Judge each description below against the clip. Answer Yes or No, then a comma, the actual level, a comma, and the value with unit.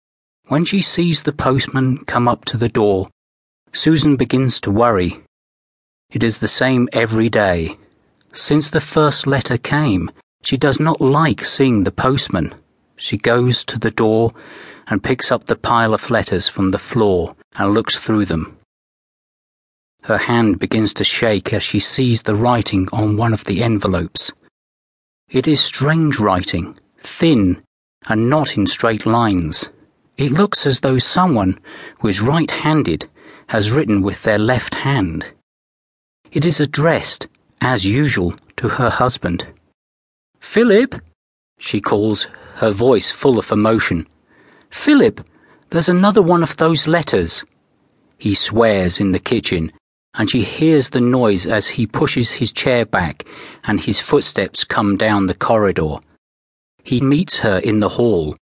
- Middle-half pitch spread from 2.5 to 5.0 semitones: No, wide, 5.6 semitones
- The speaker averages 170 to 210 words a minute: No, average, 145 wpm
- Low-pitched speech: Yes, low, 115 Hz